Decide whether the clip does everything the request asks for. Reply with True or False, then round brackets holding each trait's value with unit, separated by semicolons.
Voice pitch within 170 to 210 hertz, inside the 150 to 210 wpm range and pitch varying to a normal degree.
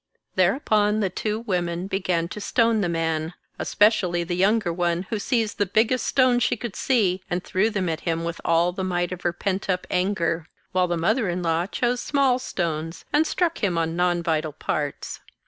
True (185 Hz; 200 wpm; 4.1 semitones)